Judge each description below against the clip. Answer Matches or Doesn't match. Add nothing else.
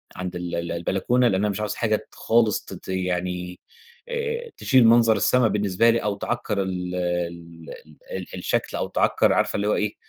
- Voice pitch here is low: Matches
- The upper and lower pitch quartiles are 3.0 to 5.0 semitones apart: Matches